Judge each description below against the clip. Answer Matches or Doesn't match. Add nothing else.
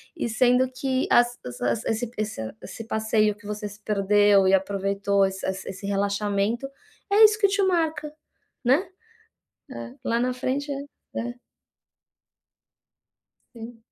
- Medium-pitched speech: Doesn't match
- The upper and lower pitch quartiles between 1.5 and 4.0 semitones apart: Doesn't match